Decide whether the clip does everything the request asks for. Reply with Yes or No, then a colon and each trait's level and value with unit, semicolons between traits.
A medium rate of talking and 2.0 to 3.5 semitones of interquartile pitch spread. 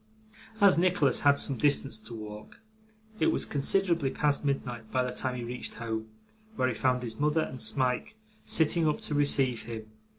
No: average, 175 wpm; average, 4.1 semitones